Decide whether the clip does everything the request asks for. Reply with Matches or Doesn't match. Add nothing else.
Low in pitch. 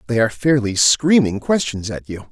Matches